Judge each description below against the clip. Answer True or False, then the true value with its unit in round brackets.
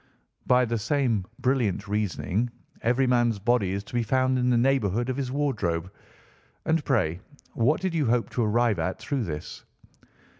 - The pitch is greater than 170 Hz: False (120 Hz)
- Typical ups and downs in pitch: True (3.9 semitones)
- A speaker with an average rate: True (165 wpm)